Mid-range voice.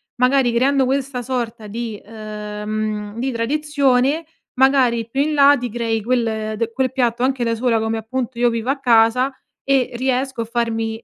No: high, 240 Hz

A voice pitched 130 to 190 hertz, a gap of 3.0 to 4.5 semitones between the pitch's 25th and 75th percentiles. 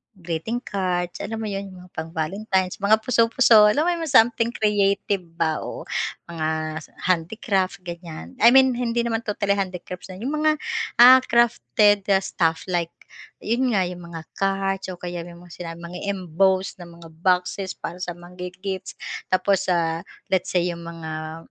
Yes: medium, 185 Hz; average, 3.5 semitones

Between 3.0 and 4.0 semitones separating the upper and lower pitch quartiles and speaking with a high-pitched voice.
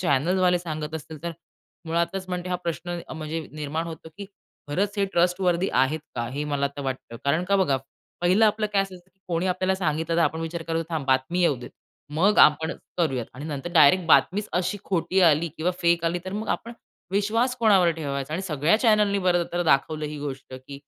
No: average, 3.7 semitones; medium, 170 Hz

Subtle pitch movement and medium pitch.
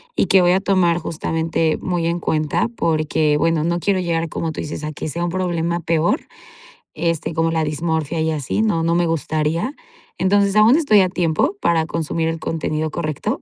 Yes: narrow, 1.8 semitones; medium, 165 Hz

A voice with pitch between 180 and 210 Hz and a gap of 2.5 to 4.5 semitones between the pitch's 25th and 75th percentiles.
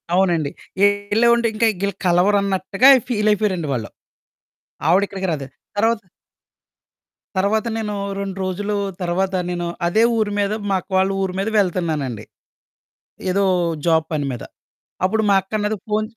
Yes: high, 195 Hz; average, 2.9 semitones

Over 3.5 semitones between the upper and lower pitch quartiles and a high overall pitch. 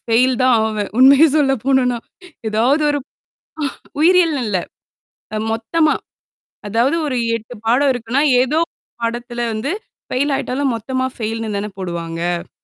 Yes: average, 3.9 semitones; high, 245 Hz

